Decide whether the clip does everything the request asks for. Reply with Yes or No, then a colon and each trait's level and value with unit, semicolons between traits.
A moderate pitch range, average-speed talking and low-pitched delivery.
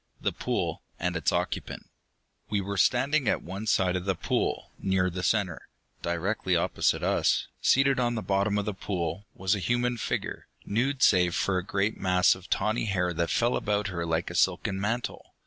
Yes: average, 3.2 semitones; average, 185 wpm; very low, 95 Hz